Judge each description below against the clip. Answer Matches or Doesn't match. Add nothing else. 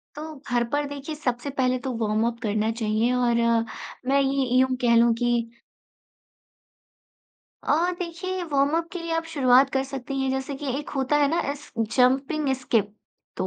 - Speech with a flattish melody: Doesn't match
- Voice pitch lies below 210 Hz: Doesn't match